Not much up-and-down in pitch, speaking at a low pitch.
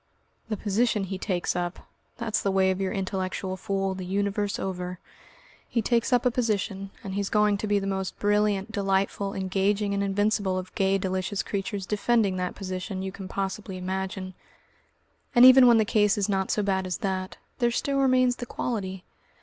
No: narrow, 1.8 semitones; high, 195 Hz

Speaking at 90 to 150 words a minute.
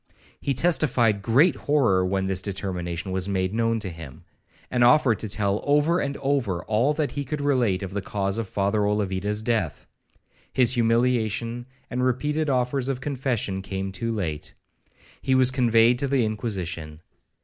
No: average, 160 wpm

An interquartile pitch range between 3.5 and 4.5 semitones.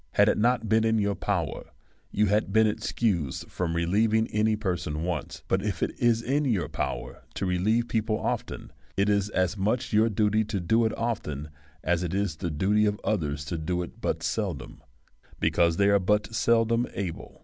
Yes: average, 3.8 semitones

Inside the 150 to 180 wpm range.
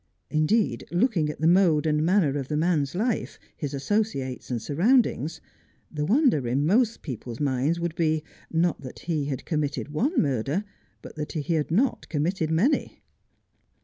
Yes: average, 160 wpm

